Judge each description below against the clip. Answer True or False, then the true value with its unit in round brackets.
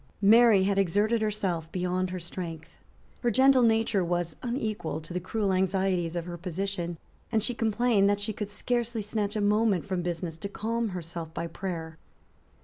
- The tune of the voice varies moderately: True (3.9 semitones)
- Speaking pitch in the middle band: False (195 Hz)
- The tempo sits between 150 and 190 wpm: True (170 wpm)